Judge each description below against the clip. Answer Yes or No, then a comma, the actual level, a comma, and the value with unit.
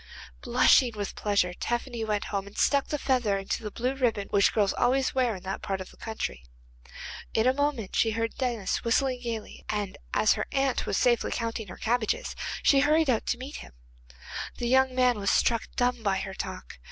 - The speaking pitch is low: No, high, 230 Hz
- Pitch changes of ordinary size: Yes, average, 3.9 semitones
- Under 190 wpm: No, average, 200 wpm